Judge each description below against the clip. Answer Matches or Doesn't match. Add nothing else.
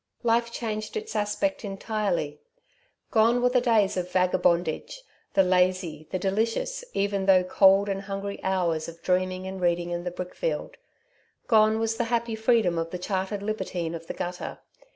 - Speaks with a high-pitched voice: Matches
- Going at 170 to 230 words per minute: Doesn't match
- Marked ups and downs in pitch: Doesn't match